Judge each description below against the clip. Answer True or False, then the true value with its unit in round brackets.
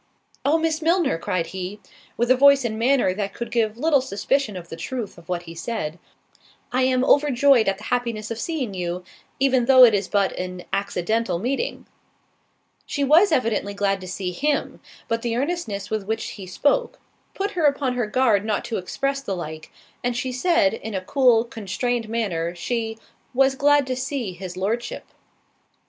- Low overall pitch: False (230 Hz)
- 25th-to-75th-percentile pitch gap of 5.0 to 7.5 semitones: True (5.5 semitones)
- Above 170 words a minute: True (180 wpm)